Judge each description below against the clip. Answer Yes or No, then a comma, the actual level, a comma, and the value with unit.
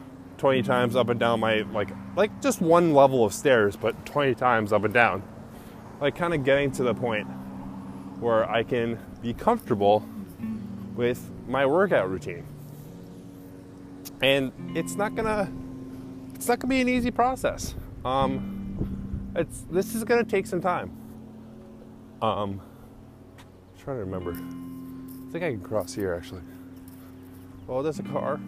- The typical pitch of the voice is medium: No, low, 115 Hz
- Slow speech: No, average, 155 wpm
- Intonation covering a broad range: Yes, wide, 6.8 semitones